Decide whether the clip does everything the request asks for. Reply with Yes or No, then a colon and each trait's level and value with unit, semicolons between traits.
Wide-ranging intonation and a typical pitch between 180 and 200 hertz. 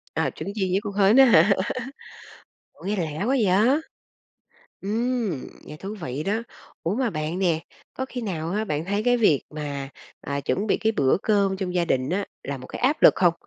Yes: wide, 5.7 semitones; high, 195 Hz